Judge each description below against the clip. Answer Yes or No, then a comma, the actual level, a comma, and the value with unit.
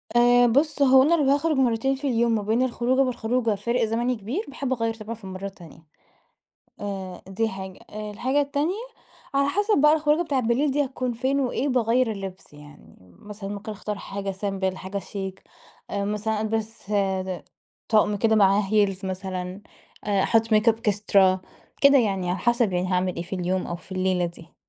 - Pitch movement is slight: No, average, 4.7 semitones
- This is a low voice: No, high, 215 Hz